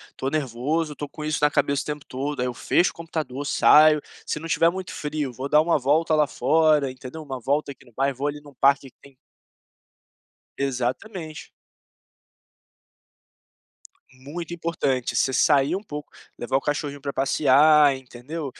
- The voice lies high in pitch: No, medium, 145 Hz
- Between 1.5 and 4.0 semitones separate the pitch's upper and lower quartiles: Yes, narrow, 2.6 semitones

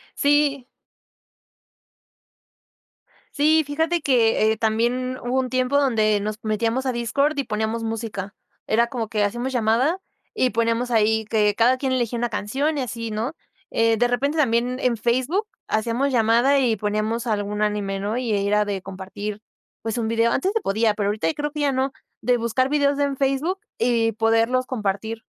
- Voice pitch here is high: Yes, high, 235 Hz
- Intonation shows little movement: No, average, 3.4 semitones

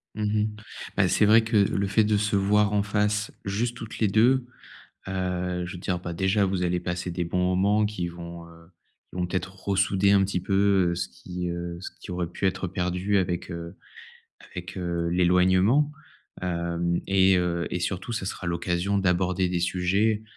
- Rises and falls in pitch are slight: Yes, narrow, 2.3 semitones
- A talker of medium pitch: No, very low, 95 Hz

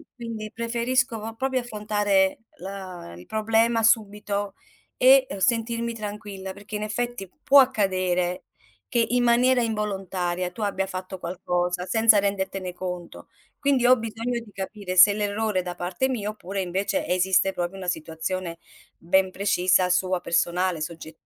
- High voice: Yes, high, 200 Hz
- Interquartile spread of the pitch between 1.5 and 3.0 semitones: No, average, 3.6 semitones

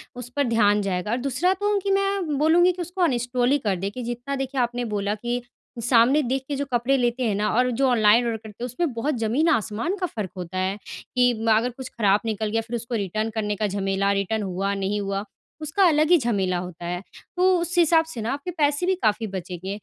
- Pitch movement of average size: No, wide, 5.8 semitones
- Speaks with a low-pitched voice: No, high, 240 Hz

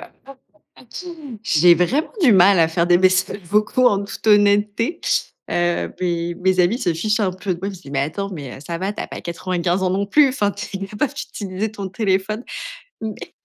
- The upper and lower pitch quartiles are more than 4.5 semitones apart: No, average, 3.1 semitones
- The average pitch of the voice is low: No, high, 195 Hz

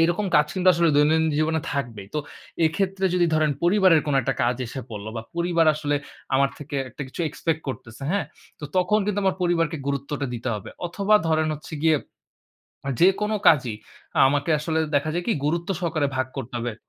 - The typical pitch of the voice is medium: Yes, medium, 155 Hz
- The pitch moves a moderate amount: Yes, average, 3.9 semitones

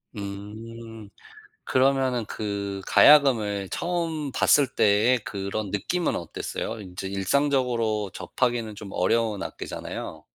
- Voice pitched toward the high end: No, low, 110 Hz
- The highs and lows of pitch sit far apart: No, average, 4.3 semitones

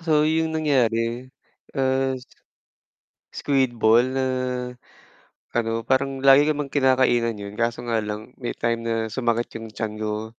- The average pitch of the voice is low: Yes, low, 120 Hz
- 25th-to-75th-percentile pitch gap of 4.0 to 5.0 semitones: No, average, 2.9 semitones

